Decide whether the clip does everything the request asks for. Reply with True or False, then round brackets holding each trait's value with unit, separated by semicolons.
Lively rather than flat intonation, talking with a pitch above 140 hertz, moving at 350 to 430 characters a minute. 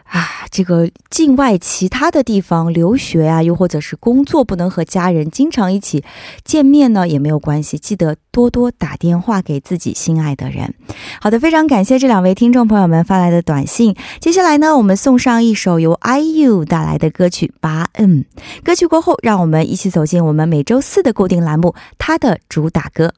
False (7.1 semitones; 185 Hz; 300 characters per minute)